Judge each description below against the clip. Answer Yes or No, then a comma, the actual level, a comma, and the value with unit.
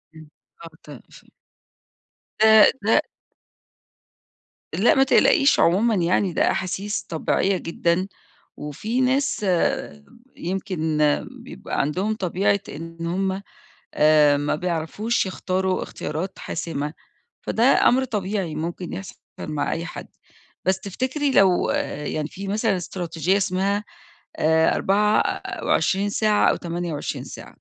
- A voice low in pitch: No, medium, 185 Hz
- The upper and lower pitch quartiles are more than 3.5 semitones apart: Yes, average, 3.9 semitones